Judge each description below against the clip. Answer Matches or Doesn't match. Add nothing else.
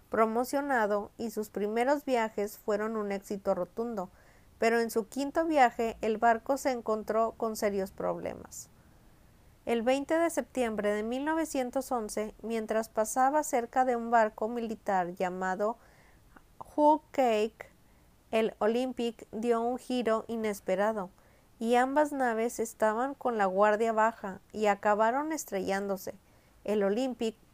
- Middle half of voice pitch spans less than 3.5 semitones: Matches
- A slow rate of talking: Matches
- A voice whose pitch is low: Doesn't match